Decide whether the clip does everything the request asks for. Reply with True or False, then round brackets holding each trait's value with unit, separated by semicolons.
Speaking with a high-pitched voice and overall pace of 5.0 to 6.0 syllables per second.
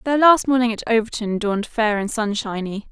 True (225 Hz; 5.5 syllables/s)